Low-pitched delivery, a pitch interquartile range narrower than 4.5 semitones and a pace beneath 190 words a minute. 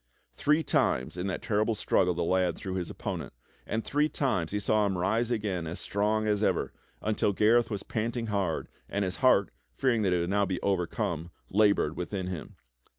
No: low, 100 Hz; average, 3.2 semitones; average, 195 wpm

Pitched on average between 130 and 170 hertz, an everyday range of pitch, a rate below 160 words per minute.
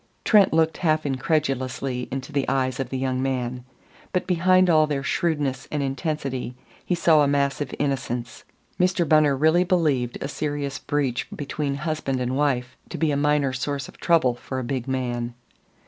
No: medium, 140 Hz; average, 3.0 semitones; average, 170 wpm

